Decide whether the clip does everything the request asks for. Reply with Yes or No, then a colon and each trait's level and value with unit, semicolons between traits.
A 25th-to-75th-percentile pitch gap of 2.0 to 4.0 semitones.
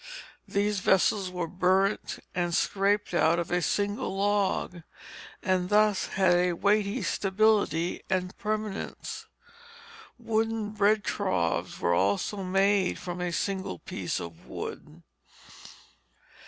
Yes: narrow, 2.6 semitones